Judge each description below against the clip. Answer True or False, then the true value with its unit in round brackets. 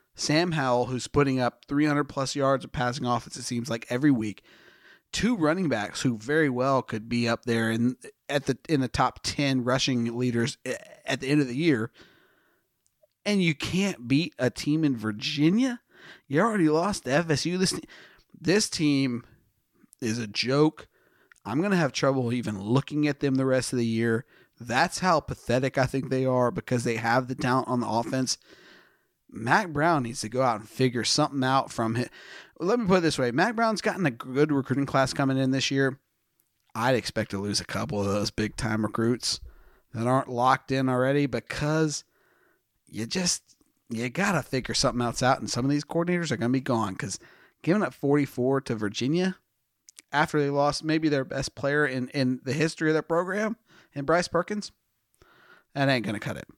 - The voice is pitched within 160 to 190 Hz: False (135 Hz)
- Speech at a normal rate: True (190 wpm)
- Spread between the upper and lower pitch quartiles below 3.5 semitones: False (3.9 semitones)